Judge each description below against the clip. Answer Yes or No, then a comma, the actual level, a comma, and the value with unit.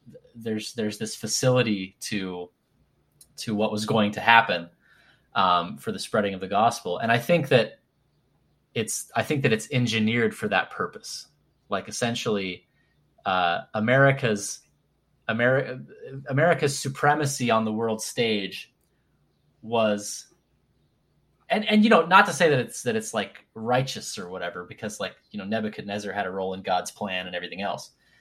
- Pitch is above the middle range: No, low, 110 Hz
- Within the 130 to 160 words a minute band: Yes, average, 155 wpm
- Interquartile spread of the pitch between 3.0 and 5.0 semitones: Yes, average, 3.6 semitones